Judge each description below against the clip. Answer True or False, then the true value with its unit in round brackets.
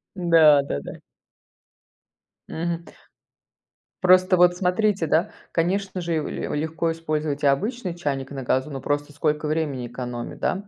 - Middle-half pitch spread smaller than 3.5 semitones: False (3.8 semitones)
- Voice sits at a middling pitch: True (160 Hz)